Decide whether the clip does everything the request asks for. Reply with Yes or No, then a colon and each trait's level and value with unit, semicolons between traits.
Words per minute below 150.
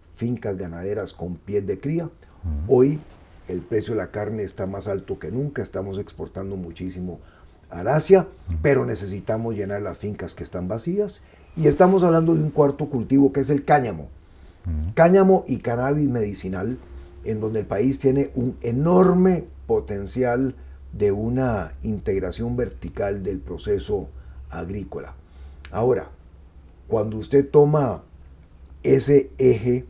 Yes: average, 130 wpm